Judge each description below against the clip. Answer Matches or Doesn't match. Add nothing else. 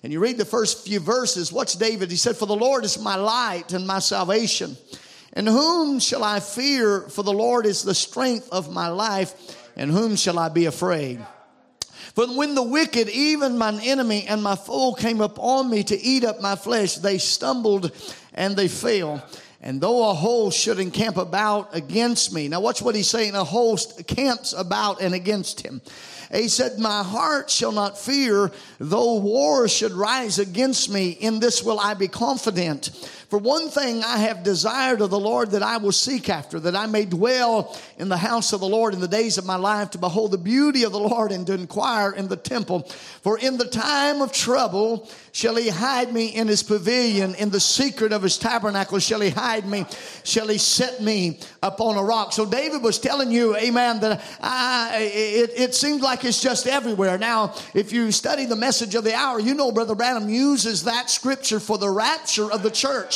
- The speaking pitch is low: Doesn't match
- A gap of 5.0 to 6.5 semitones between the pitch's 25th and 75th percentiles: Doesn't match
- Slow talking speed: Doesn't match